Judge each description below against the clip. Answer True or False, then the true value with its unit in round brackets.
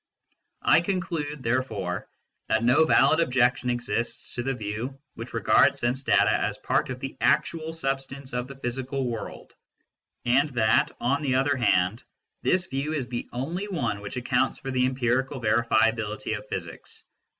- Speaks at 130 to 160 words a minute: True (155 wpm)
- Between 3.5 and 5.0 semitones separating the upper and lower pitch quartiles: False (2.6 semitones)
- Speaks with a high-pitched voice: False (130 Hz)